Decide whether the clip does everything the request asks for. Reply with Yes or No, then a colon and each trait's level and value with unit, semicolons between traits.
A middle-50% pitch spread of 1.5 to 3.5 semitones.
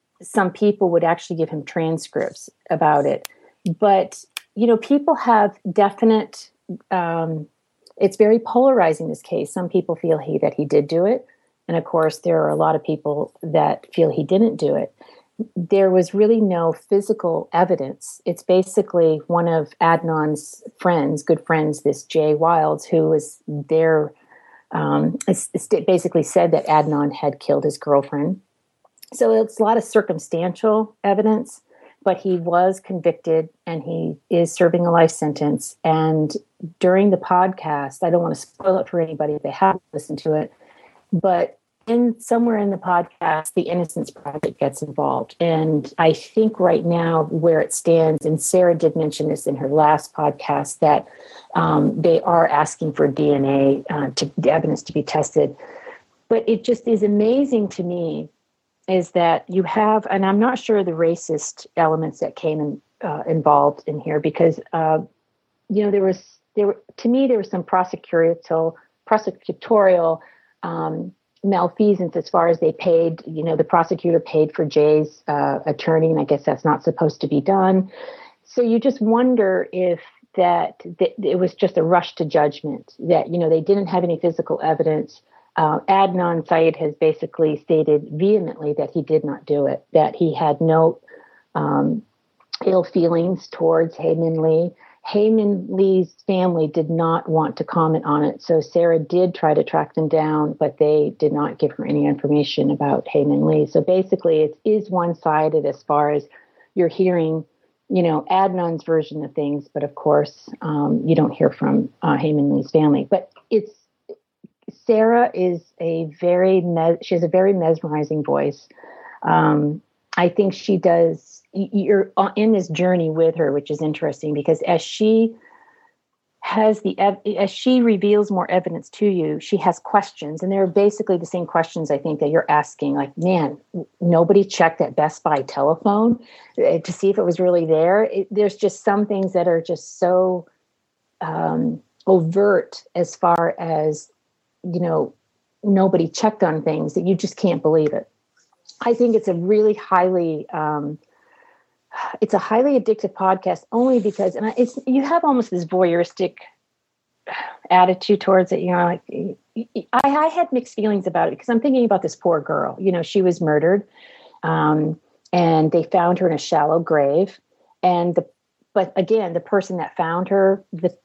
No: average, 4.1 semitones